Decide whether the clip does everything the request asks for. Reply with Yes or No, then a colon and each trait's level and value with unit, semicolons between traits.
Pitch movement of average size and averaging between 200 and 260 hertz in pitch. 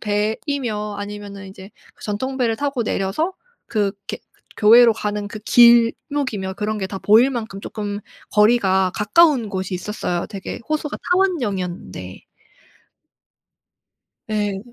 Yes: average, 3.3 semitones; high, 210 Hz